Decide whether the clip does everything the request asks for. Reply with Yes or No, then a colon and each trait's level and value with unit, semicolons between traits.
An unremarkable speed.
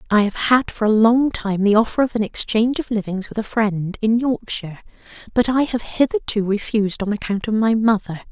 No: fast, 210 wpm